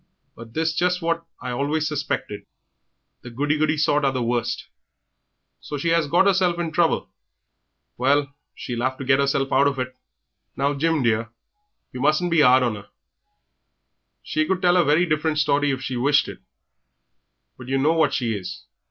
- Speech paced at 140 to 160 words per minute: No, average, 180 wpm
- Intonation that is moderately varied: Yes, average, 3.8 semitones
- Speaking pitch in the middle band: Yes, medium, 145 Hz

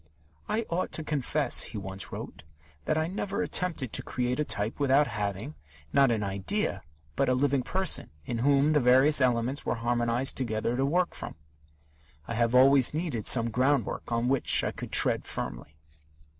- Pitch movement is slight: No, average, 4.0 semitones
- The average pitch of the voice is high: No, low, 130 Hz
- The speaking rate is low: No, average, 170 wpm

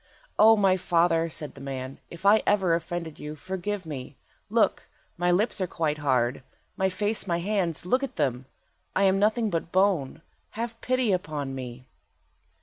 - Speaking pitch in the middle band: Yes, medium, 175 Hz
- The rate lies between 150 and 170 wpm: Yes, average, 165 wpm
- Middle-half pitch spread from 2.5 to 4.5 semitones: No, average, 5.1 semitones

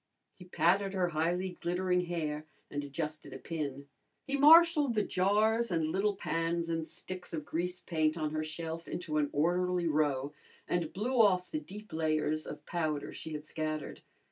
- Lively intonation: No, average, 3.1 semitones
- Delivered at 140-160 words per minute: No, average, 170 wpm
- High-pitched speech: No, medium, 170 Hz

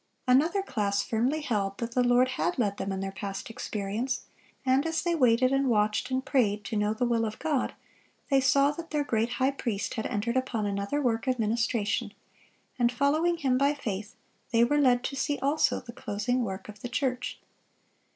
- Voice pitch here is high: Yes, high, 245 Hz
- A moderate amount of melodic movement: Yes, average, 4.4 semitones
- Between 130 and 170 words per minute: No, average, 195 wpm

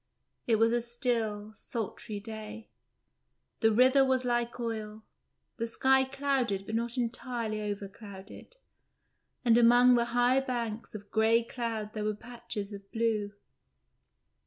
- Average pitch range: No, narrow, 2.3 semitones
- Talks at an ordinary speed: No, slow, 130 wpm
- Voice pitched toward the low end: No, high, 230 Hz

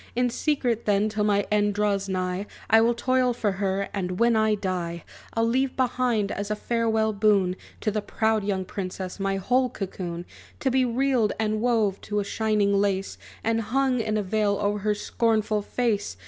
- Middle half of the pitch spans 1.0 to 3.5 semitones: Yes, narrow, 2.6 semitones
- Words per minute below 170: No, average, 185 wpm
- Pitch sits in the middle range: No, high, 210 Hz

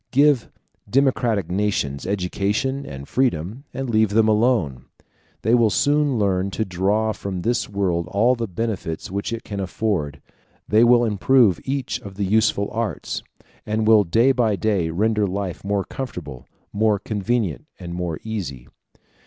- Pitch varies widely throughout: No, average, 3.9 semitones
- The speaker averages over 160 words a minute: No, average, 150 wpm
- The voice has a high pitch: No, low, 105 Hz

